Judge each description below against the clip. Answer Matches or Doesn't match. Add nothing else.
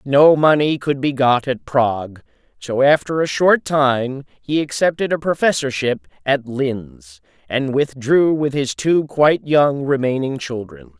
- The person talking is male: Matches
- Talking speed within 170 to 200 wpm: Doesn't match